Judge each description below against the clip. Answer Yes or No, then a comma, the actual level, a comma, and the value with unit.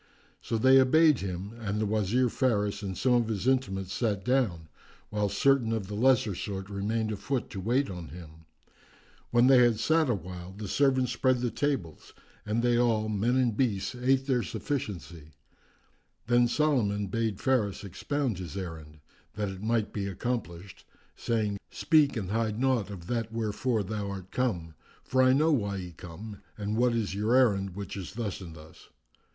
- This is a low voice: Yes, low, 110 Hz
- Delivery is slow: No, average, 175 wpm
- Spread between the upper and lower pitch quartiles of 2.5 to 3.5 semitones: No, average, 4.2 semitones